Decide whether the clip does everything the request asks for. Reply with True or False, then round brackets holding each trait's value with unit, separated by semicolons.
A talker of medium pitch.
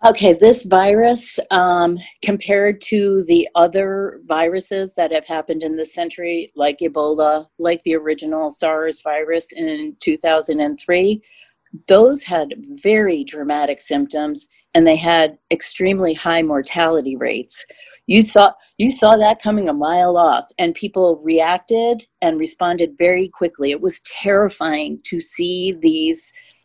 True (180 Hz)